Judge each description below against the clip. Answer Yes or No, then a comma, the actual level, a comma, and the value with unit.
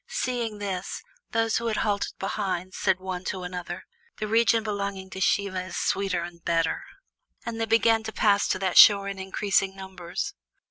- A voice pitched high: Yes, high, 195 Hz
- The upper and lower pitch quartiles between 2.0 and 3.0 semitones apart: Yes, narrow, 2.4 semitones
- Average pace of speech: Yes, average, 175 wpm